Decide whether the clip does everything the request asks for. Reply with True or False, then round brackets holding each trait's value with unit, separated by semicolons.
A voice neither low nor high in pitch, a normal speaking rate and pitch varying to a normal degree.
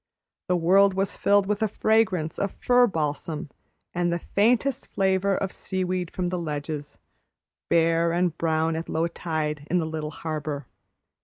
True (175 Hz; 155 wpm; 3.5 semitones)